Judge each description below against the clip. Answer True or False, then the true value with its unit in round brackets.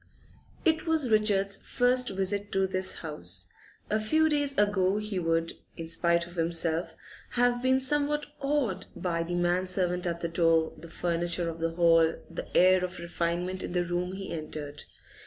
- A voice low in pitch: False (180 Hz)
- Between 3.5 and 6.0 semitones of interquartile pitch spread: True (4.0 semitones)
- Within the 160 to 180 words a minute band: True (170 wpm)